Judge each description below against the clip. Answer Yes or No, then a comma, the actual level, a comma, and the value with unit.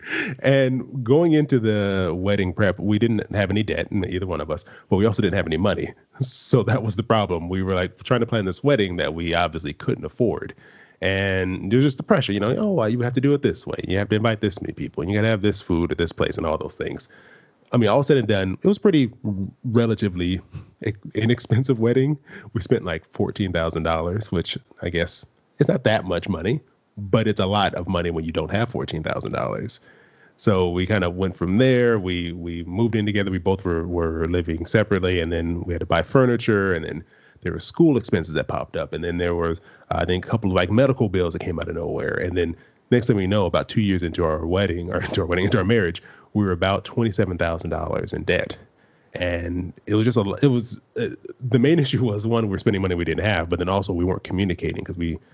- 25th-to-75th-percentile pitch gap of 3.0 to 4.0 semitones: No, average, 4.8 semitones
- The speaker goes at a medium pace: No, fast, 240 wpm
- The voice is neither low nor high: No, low, 100 Hz